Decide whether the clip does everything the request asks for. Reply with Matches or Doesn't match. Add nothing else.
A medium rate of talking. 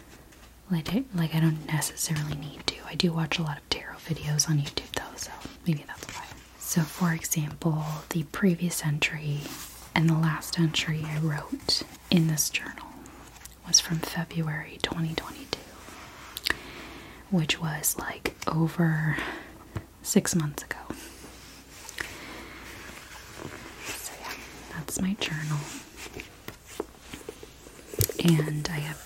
Doesn't match